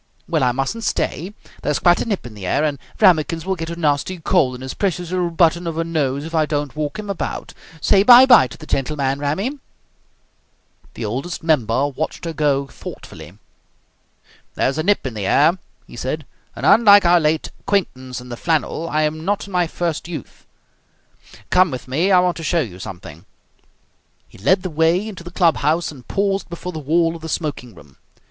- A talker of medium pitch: Yes, medium, 160 Hz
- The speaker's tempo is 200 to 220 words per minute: Yes, fast, 205 wpm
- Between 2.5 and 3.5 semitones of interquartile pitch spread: No, average, 4.4 semitones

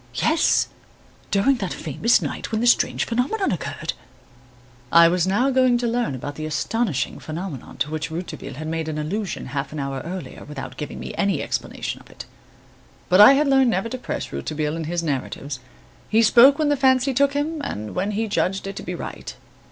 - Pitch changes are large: Yes, wide, 8.0 semitones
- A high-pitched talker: Yes, high, 195 Hz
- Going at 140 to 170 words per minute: No, average, 190 wpm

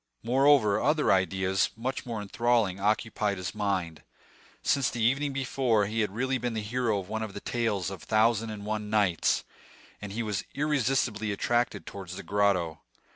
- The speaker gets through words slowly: No, average, 175 wpm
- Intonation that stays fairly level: No, average, 3.3 semitones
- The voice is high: No, low, 110 Hz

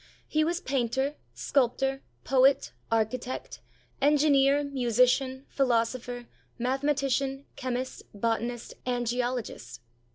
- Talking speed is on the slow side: Yes, slow, 90 wpm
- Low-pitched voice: No, very high, 255 Hz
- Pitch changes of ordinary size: No, narrow, 2.2 semitones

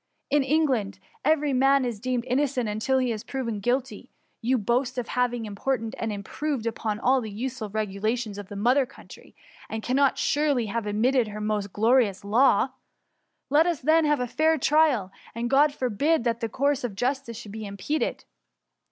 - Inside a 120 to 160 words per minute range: No, average, 180 wpm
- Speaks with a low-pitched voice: No, high, 245 Hz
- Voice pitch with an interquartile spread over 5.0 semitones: No, average, 4.0 semitones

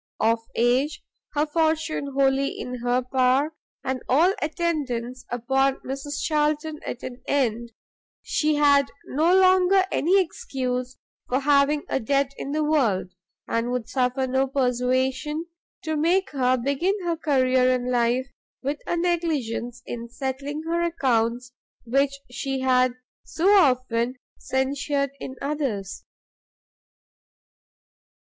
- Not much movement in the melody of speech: No, average, 3.3 semitones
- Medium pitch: No, very high, 270 Hz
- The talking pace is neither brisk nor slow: No, slow, 125 wpm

